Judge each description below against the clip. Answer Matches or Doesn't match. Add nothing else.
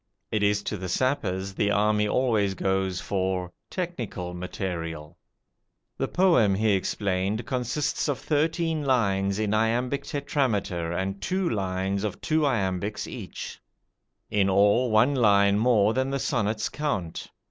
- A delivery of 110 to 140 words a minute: Matches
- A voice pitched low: Matches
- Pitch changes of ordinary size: Matches